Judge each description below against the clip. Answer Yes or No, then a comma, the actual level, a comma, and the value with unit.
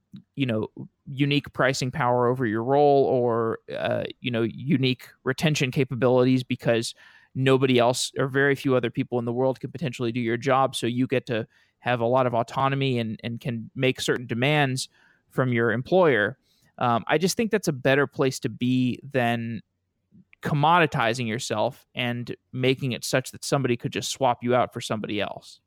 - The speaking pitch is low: Yes, low, 130 Hz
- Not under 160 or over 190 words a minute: Yes, average, 180 wpm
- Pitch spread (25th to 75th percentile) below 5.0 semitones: Yes, narrow, 2.5 semitones